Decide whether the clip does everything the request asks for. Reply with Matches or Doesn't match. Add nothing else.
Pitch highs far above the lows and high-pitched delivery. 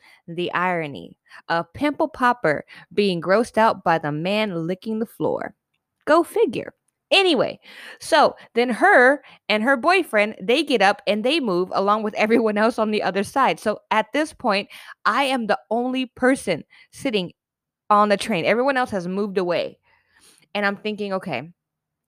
Doesn't match